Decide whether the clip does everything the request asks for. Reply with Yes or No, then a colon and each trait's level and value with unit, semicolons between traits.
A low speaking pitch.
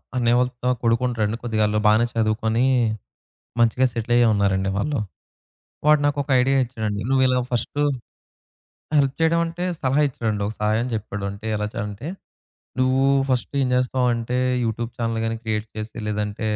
Yes: low, 115 Hz